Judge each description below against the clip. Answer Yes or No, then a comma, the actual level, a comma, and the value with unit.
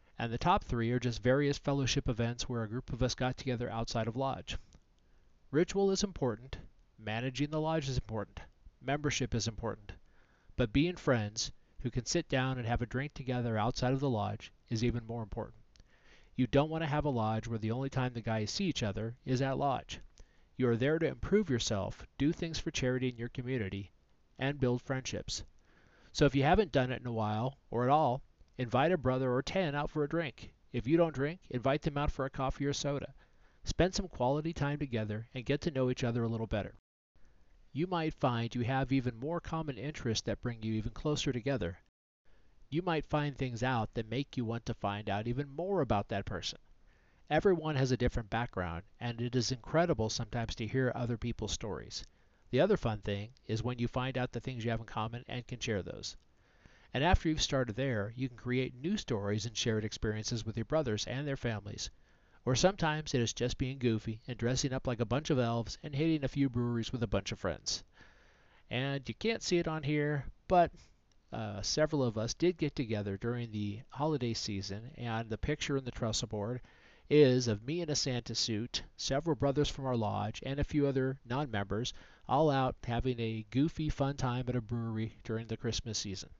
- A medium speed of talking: No, fast, 210 wpm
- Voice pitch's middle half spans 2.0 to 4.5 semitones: Yes, average, 4.0 semitones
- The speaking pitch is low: Yes, low, 125 Hz